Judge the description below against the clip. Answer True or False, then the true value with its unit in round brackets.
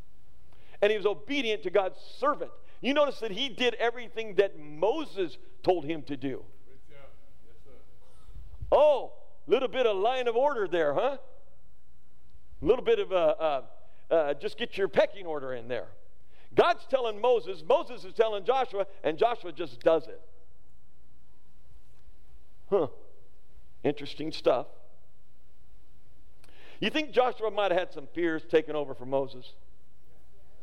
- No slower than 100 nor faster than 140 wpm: True (135 wpm)